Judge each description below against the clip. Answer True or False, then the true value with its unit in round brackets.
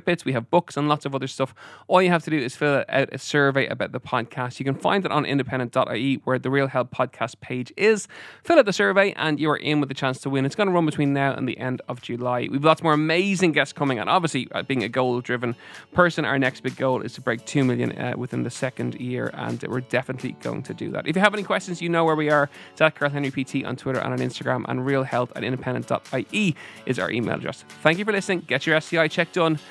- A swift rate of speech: True (255 wpm)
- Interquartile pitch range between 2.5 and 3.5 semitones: False (4.1 semitones)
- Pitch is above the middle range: False (140 Hz)